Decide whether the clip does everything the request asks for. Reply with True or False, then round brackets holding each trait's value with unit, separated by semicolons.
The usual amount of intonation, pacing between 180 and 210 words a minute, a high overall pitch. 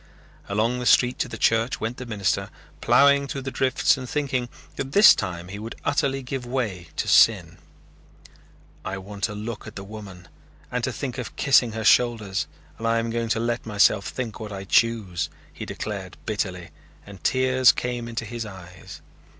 False (3.5 semitones; 185 wpm; 115 Hz)